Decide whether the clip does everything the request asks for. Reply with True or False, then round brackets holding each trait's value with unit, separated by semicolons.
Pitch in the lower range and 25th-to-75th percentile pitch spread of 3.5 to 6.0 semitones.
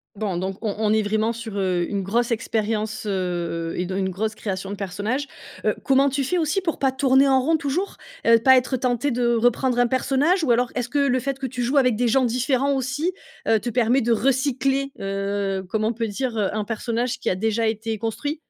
False (235 Hz; 4.1 semitones)